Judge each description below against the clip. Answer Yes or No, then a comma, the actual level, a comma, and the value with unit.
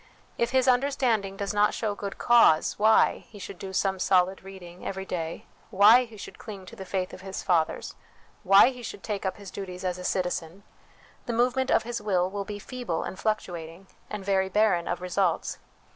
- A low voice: No, high, 195 Hz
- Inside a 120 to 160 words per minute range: No, average, 195 wpm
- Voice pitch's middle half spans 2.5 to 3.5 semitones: Yes, average, 2.8 semitones